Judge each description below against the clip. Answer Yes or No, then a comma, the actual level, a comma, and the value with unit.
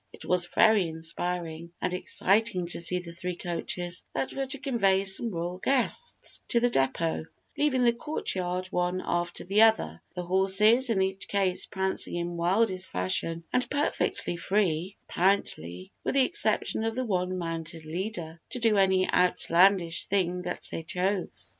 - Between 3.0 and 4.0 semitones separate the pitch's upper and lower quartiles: Yes, average, 3.6 semitones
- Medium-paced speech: Yes, average, 160 wpm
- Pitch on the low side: No, medium, 185 Hz